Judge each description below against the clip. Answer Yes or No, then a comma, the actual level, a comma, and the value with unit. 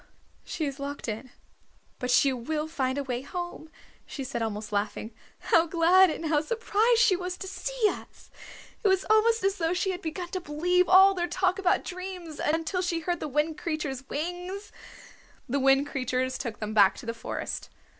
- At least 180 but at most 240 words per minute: Yes, average, 185 wpm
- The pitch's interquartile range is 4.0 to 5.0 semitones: No, wide, 5.5 semitones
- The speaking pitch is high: Yes, very high, 325 Hz